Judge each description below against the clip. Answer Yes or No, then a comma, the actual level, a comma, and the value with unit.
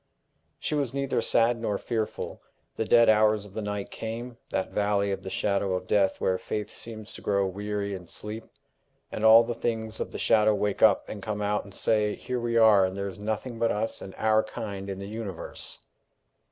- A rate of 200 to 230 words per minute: Yes, fast, 205 wpm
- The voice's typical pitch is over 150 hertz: No, low, 105 Hz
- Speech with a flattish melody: Yes, narrow, 2.0 semitones